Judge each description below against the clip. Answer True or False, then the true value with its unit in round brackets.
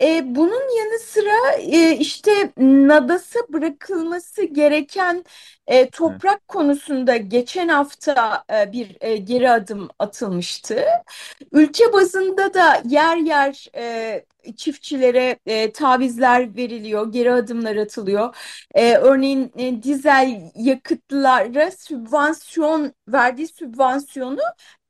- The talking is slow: True (75 wpm)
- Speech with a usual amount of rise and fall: True (4.8 semitones)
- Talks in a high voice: True (285 Hz)